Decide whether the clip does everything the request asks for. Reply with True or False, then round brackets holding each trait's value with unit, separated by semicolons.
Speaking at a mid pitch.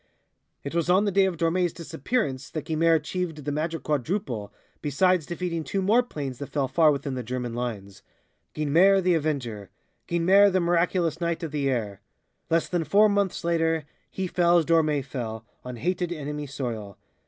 True (160 Hz)